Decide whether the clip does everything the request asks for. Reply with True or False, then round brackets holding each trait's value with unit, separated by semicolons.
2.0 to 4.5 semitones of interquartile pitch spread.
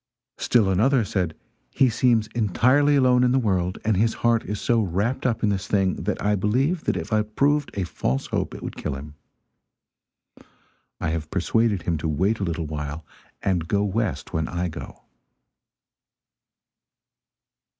False (5.2 semitones)